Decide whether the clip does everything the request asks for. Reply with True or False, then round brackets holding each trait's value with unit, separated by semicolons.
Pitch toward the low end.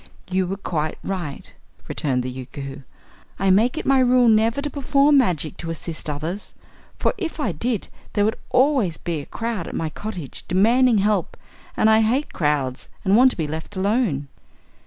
False (195 Hz)